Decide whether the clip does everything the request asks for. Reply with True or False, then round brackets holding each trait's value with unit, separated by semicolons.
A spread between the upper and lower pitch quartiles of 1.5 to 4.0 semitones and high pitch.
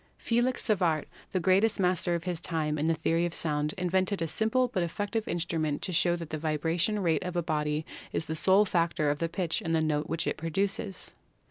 False (3.1 semitones; 170 Hz)